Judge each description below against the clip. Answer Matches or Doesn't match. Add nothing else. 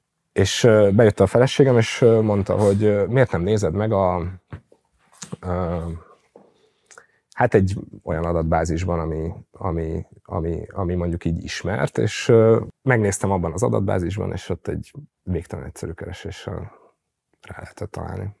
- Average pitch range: Matches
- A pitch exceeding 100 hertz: Doesn't match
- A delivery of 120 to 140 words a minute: Matches